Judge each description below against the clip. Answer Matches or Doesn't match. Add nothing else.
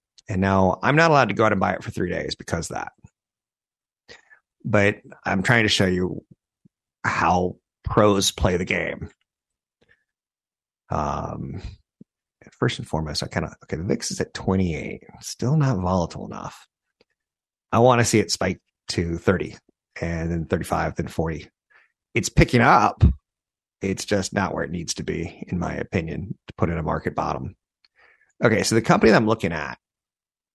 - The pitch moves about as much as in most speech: Matches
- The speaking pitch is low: Matches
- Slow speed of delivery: Doesn't match